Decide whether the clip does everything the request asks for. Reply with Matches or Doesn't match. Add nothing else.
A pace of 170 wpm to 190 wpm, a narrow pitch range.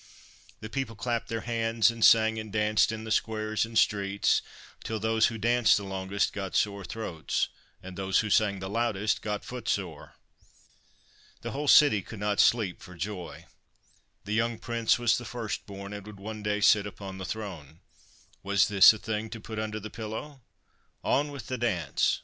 Matches